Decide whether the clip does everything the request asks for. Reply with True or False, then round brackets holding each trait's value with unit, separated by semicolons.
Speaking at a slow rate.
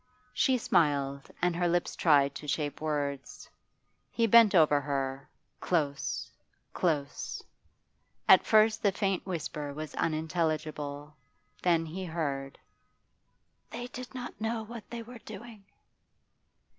True (120 wpm)